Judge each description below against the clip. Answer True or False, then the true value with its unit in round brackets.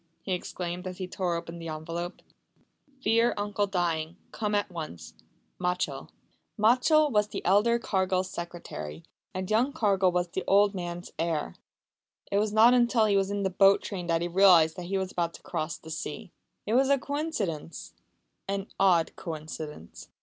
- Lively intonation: False (3.5 semitones)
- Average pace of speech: True (170 wpm)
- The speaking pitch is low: False (185 Hz)